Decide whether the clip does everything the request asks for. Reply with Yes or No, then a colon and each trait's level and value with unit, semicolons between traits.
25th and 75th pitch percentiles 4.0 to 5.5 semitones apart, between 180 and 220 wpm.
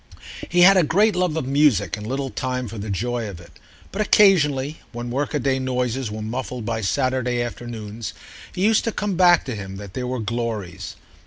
Yes: average, 5.1 semitones; average, 190 wpm